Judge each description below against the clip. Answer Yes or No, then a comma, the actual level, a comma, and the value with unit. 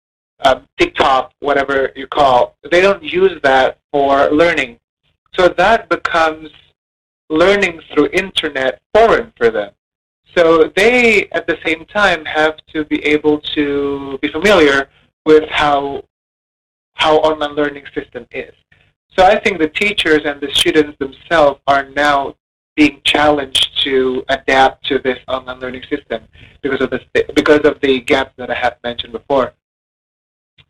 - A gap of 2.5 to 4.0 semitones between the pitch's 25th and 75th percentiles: Yes, average, 3.4 semitones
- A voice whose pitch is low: No, medium, 150 Hz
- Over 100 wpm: Yes, average, 135 wpm